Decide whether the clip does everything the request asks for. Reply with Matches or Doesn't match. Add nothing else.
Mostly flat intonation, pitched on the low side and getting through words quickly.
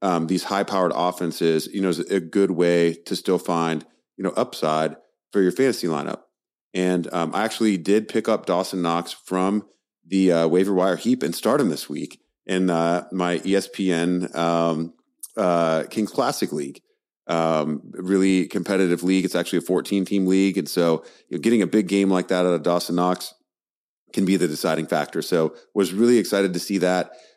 Doesn't match